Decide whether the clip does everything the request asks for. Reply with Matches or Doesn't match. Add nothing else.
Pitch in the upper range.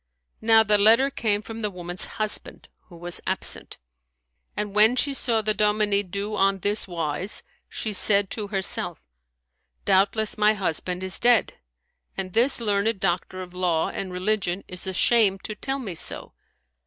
Matches